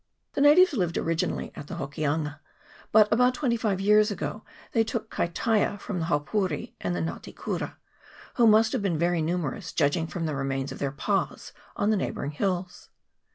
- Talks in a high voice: No, medium, 180 Hz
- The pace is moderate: Yes, average, 180 wpm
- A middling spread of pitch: No, wide, 6.1 semitones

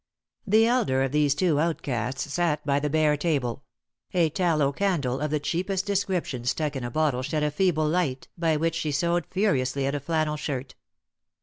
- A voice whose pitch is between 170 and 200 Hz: No, medium, 150 Hz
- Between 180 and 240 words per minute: Yes, average, 185 wpm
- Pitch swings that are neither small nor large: Yes, average, 3.7 semitones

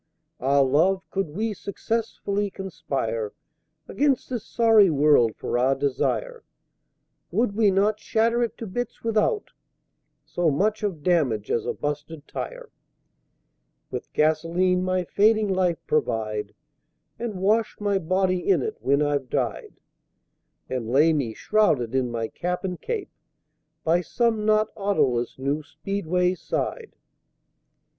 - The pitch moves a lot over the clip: Yes, wide, 6.8 semitones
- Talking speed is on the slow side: Yes, slow, 130 wpm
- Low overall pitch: No, medium, 185 Hz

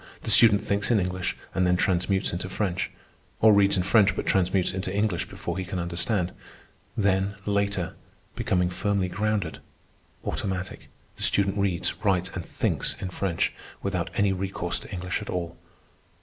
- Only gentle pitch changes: Yes, narrow, 1.9 semitones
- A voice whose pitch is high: No, very low, 95 Hz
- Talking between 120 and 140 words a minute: No, average, 160 wpm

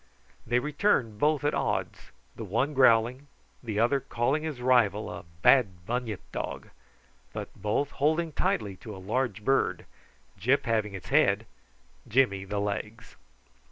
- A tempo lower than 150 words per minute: Yes, average, 140 wpm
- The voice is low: Yes, low, 120 Hz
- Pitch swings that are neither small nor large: Yes, average, 4.6 semitones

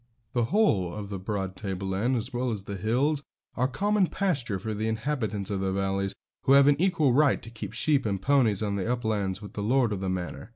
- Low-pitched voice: Yes, low, 110 Hz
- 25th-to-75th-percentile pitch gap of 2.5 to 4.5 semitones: No, average, 5.3 semitones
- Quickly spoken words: Yes, fast, 220 wpm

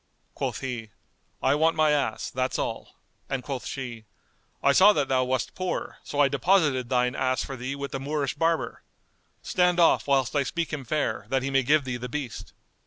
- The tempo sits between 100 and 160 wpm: No, average, 195 wpm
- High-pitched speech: No, low, 135 Hz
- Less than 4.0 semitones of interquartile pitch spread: Yes, average, 2.9 semitones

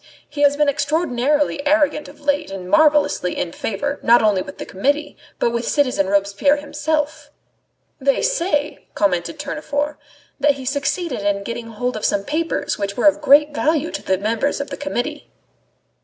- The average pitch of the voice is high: Yes, very high, 285 Hz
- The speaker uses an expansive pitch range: No, average, 4.9 semitones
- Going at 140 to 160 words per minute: No, average, 170 wpm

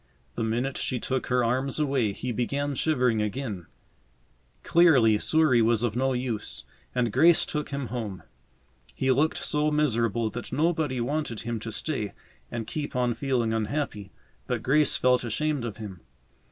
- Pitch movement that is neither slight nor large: Yes, average, 4.0 semitones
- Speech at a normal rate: Yes, average, 155 wpm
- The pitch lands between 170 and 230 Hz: No, low, 125 Hz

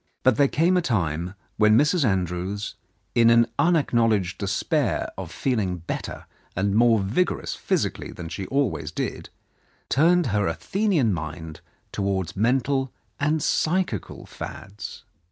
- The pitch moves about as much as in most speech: No, wide, 6.7 semitones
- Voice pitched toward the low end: Yes, low, 110 Hz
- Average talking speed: No, slow, 125 wpm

